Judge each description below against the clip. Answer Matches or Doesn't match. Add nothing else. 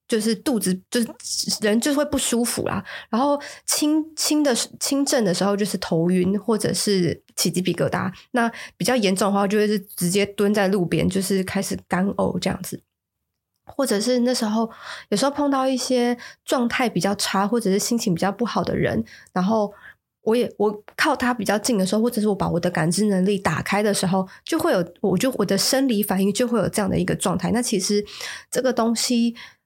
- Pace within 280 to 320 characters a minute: Matches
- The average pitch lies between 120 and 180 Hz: Doesn't match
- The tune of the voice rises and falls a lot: Doesn't match